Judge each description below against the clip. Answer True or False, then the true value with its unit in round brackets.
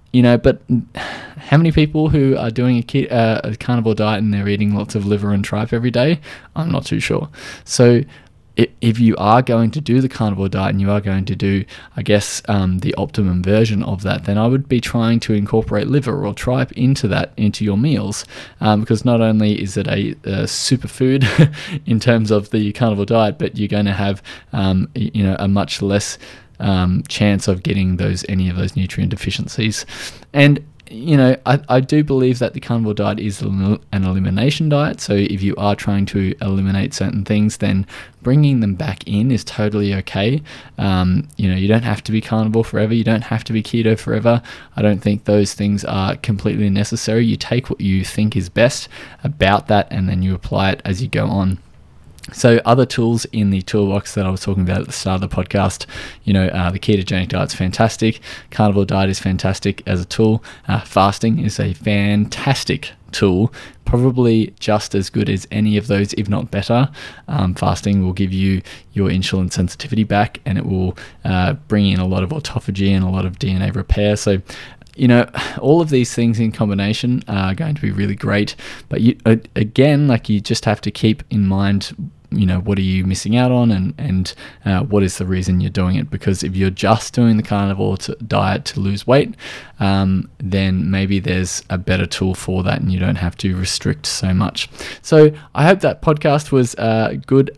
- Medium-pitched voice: False (105 Hz)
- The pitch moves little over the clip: False (3.5 semitones)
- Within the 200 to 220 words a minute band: True (205 wpm)